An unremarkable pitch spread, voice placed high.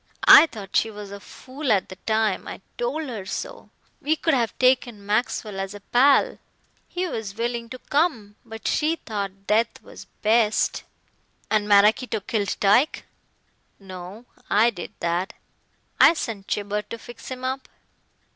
Yes: average, 4.0 semitones; high, 220 Hz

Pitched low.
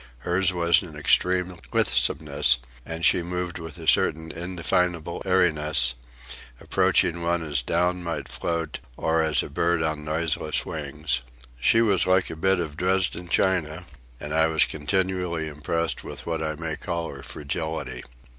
Yes: very low, 85 Hz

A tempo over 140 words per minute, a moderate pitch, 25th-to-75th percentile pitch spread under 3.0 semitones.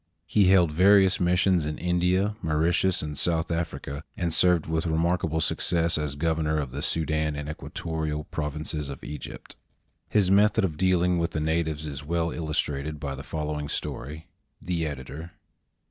No: average, 155 wpm; very low, 80 Hz; narrow, 2.6 semitones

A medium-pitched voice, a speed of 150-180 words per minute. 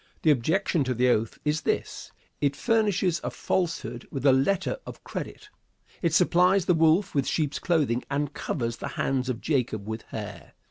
Yes: medium, 150 Hz; average, 175 wpm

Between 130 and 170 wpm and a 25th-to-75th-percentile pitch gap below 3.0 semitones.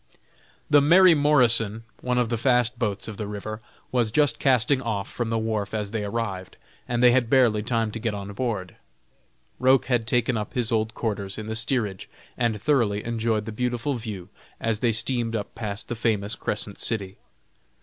No: average, 185 wpm; narrow, 2.6 semitones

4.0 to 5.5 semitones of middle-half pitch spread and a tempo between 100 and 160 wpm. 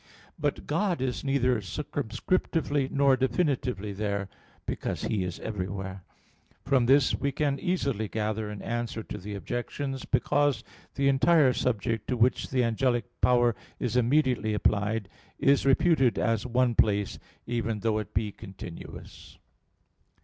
Yes: average, 4.3 semitones; slow, 135 wpm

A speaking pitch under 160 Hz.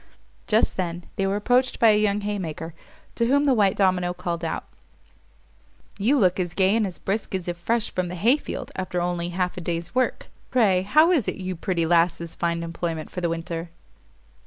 No: medium, 185 Hz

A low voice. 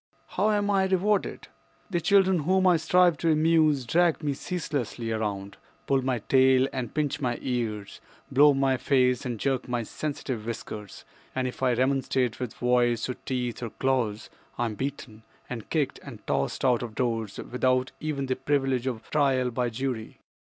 Yes: low, 130 Hz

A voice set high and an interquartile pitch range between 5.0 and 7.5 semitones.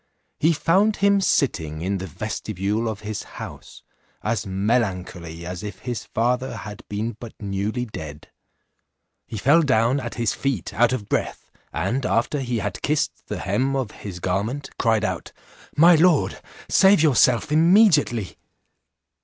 No: low, 115 Hz; wide, 5.6 semitones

